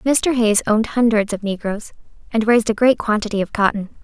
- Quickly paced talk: No, average, 195 wpm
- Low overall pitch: No, high, 220 Hz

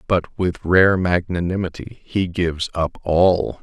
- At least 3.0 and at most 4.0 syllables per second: Yes, 3.9 syllables/s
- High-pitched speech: No, very low, 90 Hz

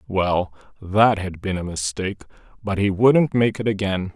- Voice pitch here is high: No, low, 100 Hz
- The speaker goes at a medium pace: Yes, average, 175 wpm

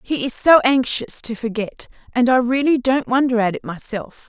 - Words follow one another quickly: No, average, 195 wpm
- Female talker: Yes, female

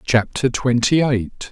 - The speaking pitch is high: No, low, 125 Hz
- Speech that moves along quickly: No, slow, 120 wpm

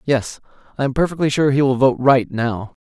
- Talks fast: Yes, fast, 210 wpm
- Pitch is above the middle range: No, low, 130 Hz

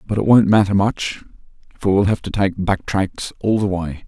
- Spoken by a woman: No, male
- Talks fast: Yes, fast, 220 wpm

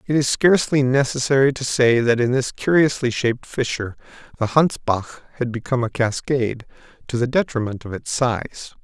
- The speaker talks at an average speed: Yes, average, 165 wpm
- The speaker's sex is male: Yes, male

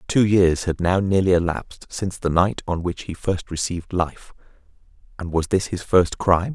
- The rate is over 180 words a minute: Yes, average, 190 wpm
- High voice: No, very low, 90 Hz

